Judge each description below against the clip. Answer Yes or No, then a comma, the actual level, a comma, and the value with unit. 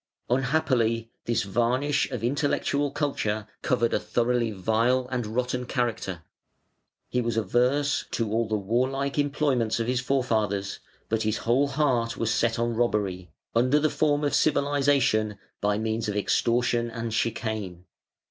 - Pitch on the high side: No, low, 120 Hz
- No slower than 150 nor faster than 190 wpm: No, average, 140 wpm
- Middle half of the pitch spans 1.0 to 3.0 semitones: No, average, 3.4 semitones